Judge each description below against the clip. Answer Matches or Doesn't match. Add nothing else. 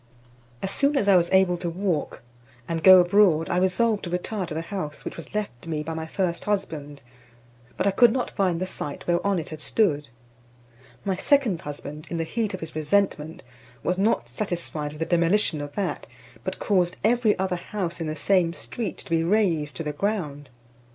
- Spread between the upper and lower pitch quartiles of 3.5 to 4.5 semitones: Matches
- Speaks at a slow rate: Doesn't match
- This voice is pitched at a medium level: Matches